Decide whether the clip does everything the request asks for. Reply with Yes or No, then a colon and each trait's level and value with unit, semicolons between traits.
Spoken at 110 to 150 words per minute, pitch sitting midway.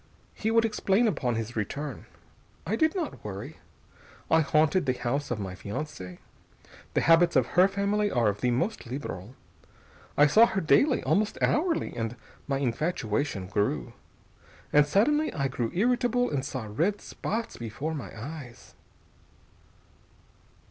Yes: average, 140 wpm; medium, 145 Hz